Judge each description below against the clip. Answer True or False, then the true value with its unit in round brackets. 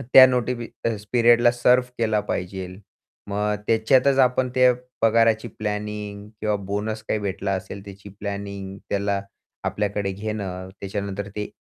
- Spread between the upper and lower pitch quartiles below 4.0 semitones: True (2.5 semitones)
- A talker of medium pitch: False (105 Hz)